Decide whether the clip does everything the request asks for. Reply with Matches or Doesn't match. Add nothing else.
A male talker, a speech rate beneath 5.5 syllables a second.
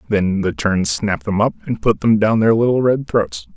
Matches